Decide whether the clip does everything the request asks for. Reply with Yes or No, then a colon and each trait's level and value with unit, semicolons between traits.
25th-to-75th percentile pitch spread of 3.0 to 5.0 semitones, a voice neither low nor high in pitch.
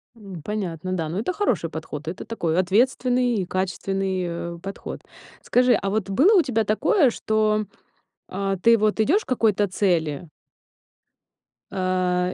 No: average, 3.9 semitones; high, 195 Hz